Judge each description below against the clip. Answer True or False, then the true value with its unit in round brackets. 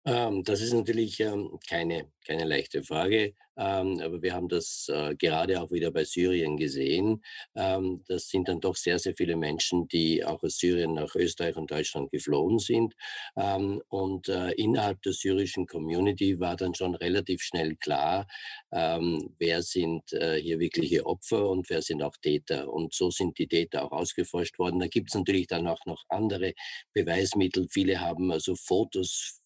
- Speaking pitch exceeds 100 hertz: False (90 Hz)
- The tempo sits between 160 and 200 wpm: True (175 wpm)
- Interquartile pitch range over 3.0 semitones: False (2.4 semitones)